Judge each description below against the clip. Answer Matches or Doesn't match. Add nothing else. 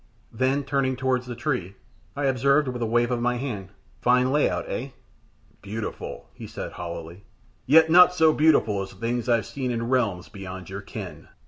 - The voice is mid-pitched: Doesn't match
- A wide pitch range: Doesn't match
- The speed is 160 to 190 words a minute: Matches